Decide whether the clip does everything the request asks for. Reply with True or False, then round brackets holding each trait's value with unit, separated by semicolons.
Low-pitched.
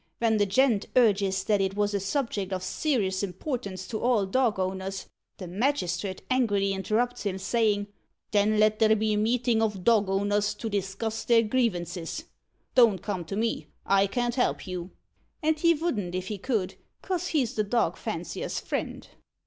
False (210 Hz)